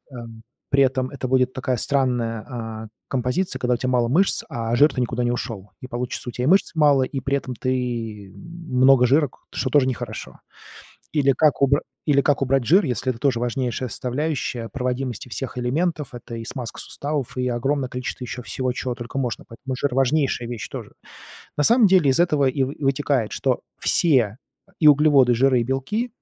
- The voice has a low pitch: Yes, low, 130 Hz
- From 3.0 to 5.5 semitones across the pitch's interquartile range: No, narrow, 2.5 semitones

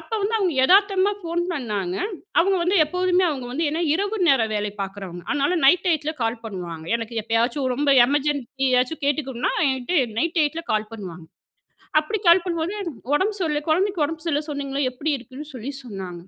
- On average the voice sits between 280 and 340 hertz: Yes, very high, 290 Hz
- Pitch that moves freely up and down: Yes, wide, 6.4 semitones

